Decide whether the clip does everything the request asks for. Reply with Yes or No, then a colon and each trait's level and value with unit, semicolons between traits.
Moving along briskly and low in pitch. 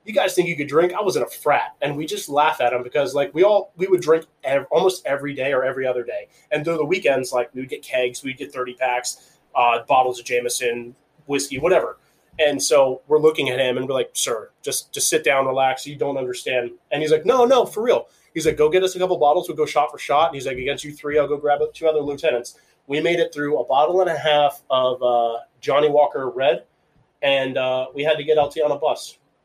No: fast, 255 wpm; medium, 150 Hz